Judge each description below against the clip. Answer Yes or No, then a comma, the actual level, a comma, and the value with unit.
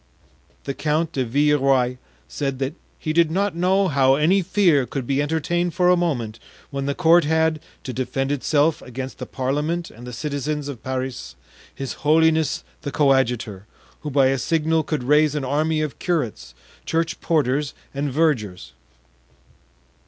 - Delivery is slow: No, average, 155 wpm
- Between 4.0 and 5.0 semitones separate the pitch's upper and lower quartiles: No, average, 3.5 semitones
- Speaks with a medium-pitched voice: Yes, medium, 145 Hz